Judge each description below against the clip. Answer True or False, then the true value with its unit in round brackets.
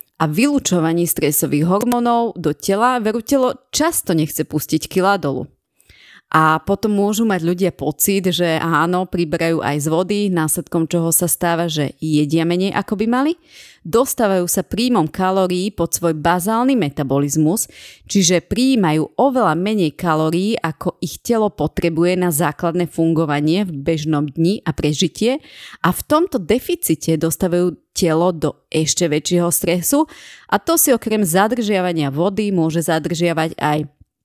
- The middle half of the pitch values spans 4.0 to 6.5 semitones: True (4.5 semitones)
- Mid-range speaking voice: True (175 Hz)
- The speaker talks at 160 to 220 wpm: False (135 wpm)